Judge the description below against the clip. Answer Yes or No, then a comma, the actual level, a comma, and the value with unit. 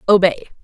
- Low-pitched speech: No, medium, 185 Hz